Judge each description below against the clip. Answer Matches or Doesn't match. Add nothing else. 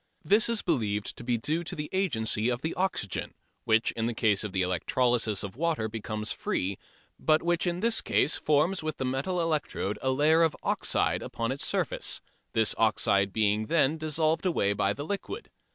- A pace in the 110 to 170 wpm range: Doesn't match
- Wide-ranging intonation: Matches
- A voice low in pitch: Matches